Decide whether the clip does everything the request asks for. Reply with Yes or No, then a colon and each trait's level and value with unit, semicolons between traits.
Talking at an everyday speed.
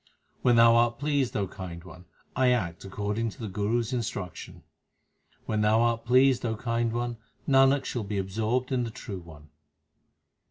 Yes: average, 170 wpm